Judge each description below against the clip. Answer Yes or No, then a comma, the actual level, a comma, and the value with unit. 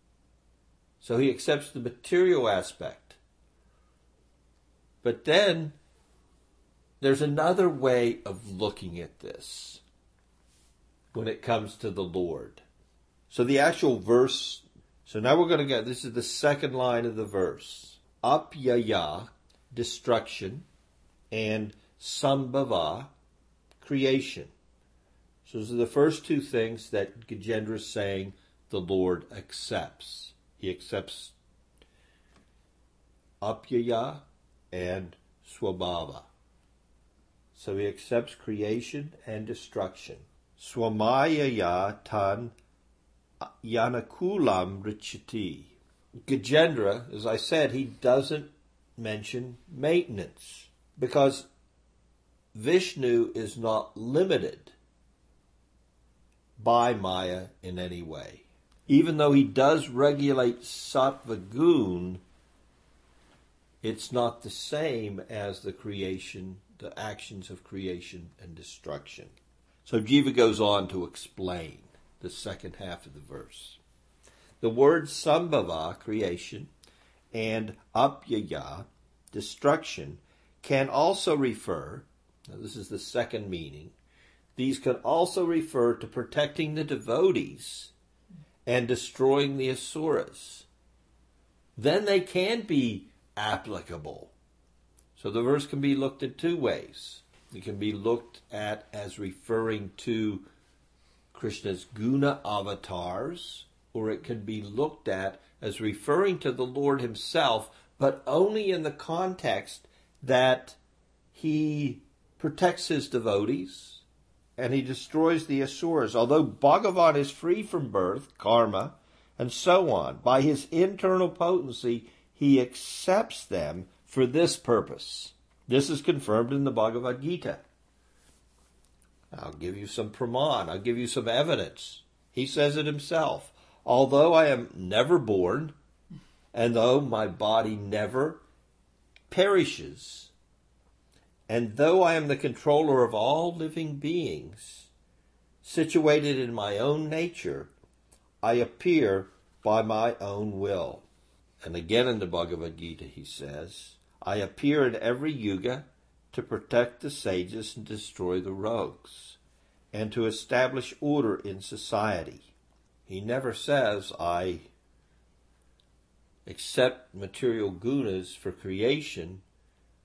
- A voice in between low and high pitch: No, low, 110 Hz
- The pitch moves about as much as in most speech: No, wide, 8.7 semitones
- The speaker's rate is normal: No, slow, 110 wpm